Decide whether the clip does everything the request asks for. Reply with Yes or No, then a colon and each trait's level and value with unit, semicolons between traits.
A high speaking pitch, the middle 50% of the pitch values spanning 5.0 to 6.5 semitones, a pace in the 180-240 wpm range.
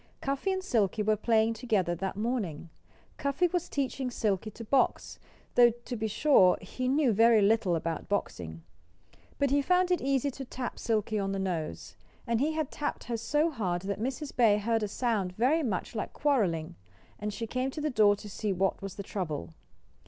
Yes: high, 225 Hz; wide, 5.4 semitones; average, 190 wpm